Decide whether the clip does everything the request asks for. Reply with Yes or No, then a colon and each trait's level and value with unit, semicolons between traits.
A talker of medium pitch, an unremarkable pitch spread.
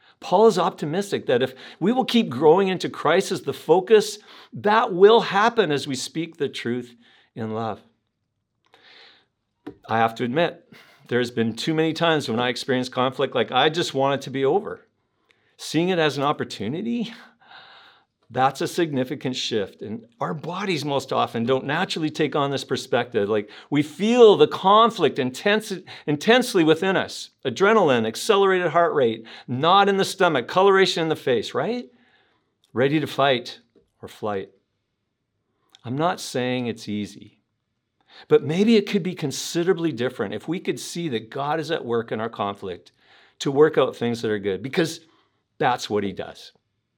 No: medium, 150 Hz; wide, 6.6 semitones